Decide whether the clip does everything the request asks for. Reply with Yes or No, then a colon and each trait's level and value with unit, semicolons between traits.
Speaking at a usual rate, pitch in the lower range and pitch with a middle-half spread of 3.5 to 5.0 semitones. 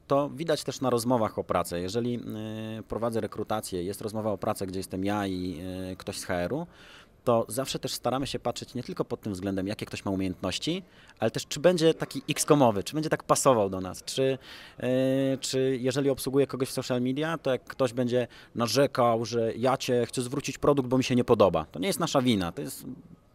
No: fast, 205 wpm; low, 125 Hz; average, 3.9 semitones